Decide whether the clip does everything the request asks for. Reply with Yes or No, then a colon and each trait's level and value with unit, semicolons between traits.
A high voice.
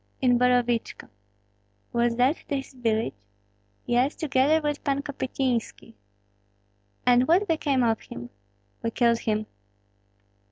Yes: very high, 250 Hz